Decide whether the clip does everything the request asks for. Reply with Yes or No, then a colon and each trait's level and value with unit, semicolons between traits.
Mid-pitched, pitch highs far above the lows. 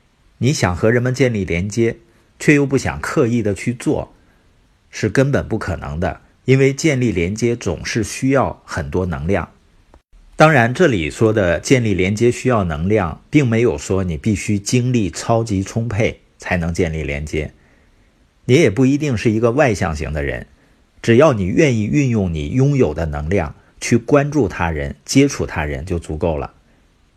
No: low, 105 Hz; wide, 6.7 semitones